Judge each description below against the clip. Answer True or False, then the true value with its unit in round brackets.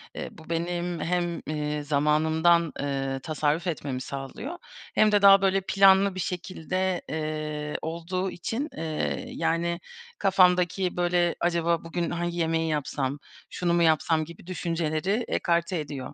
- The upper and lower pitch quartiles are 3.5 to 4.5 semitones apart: False (2.7 semitones)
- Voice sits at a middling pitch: True (170 Hz)